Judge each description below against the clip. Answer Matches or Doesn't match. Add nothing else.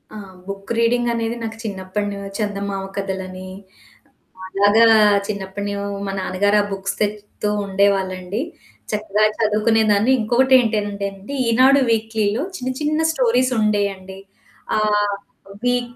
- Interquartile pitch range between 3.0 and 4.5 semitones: Doesn't match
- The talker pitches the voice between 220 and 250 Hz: Doesn't match